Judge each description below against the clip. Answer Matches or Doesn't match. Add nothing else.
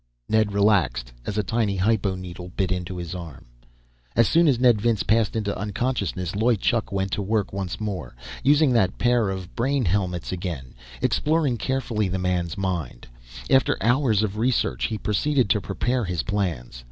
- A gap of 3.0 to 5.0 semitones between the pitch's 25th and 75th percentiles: Matches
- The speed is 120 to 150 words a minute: Doesn't match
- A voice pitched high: Doesn't match